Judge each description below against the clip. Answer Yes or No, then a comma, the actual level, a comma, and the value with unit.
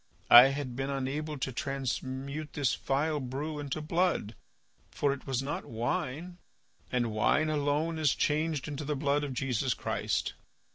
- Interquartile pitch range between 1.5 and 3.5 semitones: Yes, narrow, 2.5 semitones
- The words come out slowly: No, average, 150 wpm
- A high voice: No, medium, 140 Hz